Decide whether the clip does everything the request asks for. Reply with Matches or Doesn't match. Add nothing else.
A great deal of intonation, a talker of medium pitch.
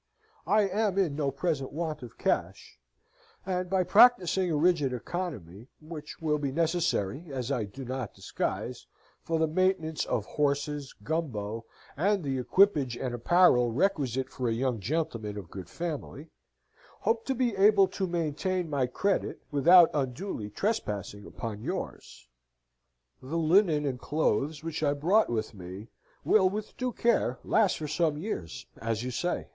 Matches